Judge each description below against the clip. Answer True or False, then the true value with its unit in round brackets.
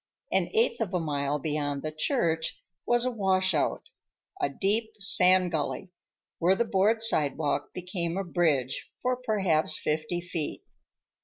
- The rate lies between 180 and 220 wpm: False (140 wpm)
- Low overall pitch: False (175 Hz)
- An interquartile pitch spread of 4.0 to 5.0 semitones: True (4.7 semitones)